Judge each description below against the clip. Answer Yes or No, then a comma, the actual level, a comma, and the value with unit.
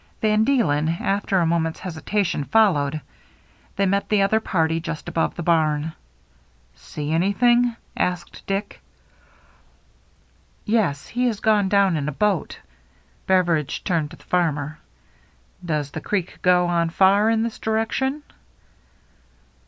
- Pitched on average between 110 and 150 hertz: No, medium, 180 Hz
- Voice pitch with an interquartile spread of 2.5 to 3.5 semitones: No, average, 4.7 semitones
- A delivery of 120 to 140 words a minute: Yes, slow, 135 wpm